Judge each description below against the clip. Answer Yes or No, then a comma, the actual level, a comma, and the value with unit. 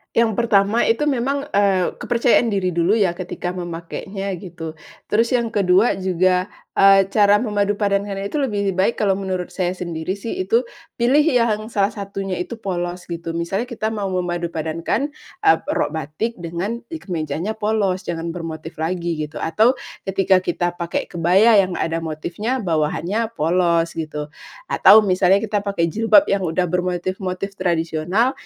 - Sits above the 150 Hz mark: Yes, high, 190 Hz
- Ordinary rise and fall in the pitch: Yes, average, 3.8 semitones